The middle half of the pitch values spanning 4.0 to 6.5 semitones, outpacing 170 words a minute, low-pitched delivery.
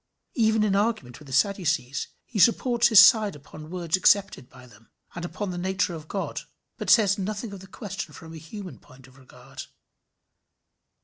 No: average, 5.1 semitones; average, 180 wpm; medium, 185 Hz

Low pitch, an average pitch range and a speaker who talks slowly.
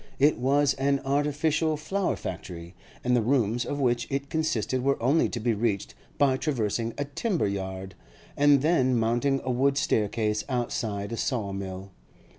No: low, 125 Hz; average, 4.6 semitones; average, 160 wpm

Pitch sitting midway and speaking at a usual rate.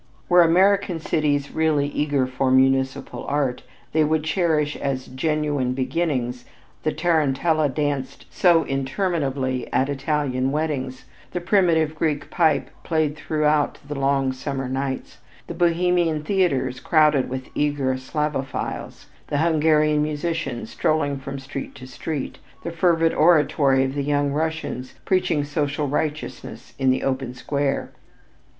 No: medium, 145 Hz; slow, 130 wpm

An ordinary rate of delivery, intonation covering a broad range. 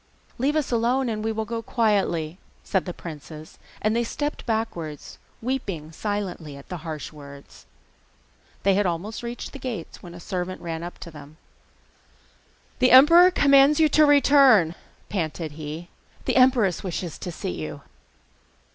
Yes: average, 150 wpm; wide, 7.4 semitones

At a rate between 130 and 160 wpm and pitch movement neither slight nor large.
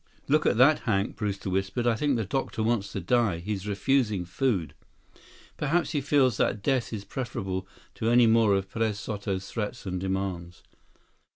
No: average, 170 wpm; average, 4.1 semitones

